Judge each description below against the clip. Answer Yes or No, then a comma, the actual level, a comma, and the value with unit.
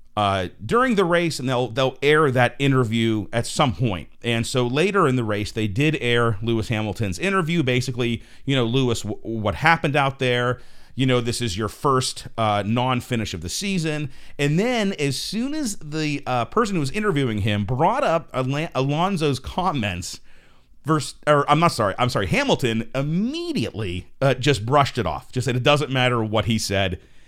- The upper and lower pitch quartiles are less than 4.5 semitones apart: No, average, 4.8 semitones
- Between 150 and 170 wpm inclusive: No, average, 185 wpm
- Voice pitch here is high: No, low, 125 Hz